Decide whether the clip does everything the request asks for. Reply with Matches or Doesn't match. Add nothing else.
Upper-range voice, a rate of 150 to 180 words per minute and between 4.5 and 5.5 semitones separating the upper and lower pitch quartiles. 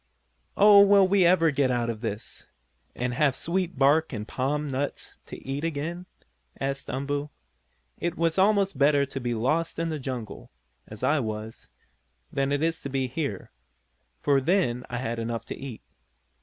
Doesn't match